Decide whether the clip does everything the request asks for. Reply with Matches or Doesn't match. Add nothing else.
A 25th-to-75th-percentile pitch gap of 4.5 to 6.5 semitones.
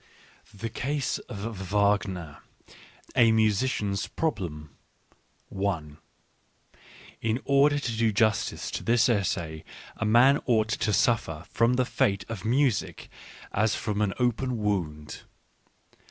Doesn't match